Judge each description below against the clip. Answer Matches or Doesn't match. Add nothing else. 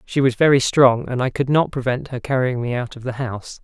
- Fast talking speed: Matches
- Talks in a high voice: Doesn't match